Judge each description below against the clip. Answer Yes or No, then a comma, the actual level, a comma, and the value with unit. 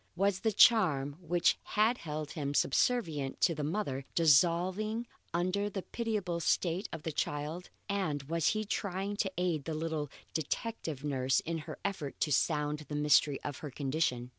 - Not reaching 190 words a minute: Yes, average, 165 wpm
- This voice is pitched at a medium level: Yes, medium, 165 Hz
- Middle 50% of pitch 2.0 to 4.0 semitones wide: No, average, 4.8 semitones